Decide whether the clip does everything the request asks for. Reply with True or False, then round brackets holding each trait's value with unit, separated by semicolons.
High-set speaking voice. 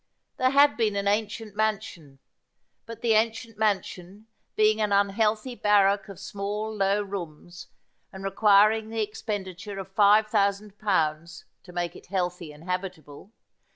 True (200 Hz)